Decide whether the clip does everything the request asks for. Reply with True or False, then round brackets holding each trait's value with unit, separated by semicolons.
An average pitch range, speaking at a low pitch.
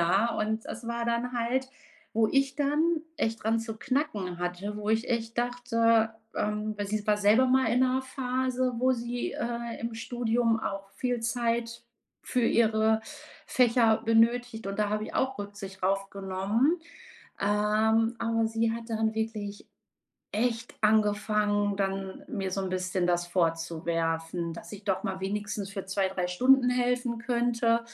False (3.0 semitones; 225 Hz)